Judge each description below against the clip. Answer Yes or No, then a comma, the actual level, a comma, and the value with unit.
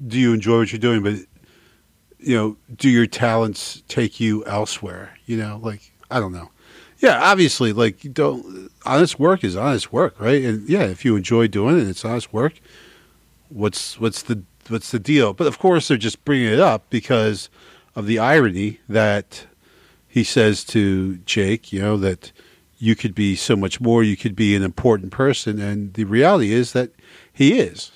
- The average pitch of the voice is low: Yes, low, 115 Hz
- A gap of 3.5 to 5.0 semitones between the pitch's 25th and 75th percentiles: No, average, 3.1 semitones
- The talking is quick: No, average, 185 wpm